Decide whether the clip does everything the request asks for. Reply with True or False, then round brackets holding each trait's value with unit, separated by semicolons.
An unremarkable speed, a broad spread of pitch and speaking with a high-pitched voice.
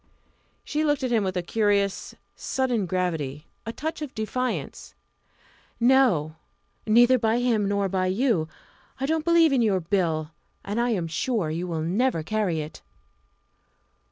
True (150 wpm; 6.3 semitones; 210 Hz)